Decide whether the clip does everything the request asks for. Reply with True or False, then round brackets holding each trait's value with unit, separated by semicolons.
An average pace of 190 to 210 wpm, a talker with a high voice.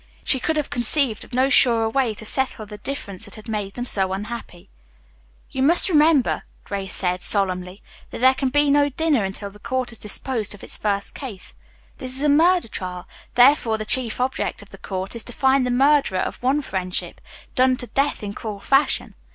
True (200 wpm; 240 Hz)